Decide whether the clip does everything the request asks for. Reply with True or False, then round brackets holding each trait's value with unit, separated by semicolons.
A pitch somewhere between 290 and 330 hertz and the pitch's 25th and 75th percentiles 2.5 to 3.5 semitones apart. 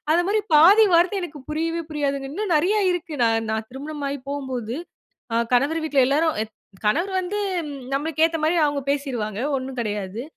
False (295 Hz; 4.2 semitones)